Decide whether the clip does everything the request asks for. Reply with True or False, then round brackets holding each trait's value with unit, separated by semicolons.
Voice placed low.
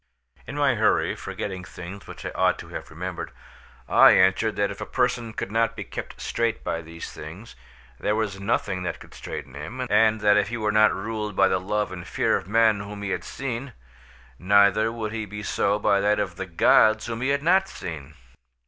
True (105 Hz)